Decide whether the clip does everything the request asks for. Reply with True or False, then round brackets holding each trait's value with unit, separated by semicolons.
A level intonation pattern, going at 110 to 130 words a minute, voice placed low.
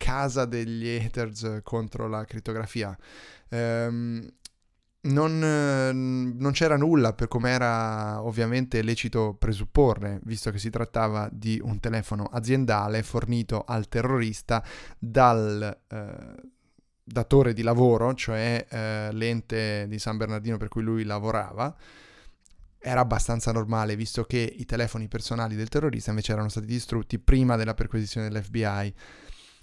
True (1.8 semitones; 125 wpm; 115 Hz)